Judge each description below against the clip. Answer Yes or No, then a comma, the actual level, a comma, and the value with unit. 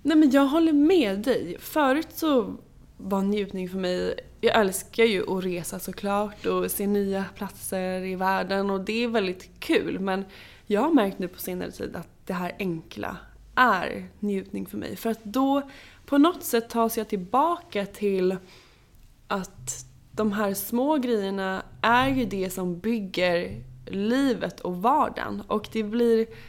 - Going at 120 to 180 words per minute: Yes, average, 160 wpm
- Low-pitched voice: No, high, 205 Hz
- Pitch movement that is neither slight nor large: Yes, average, 4.2 semitones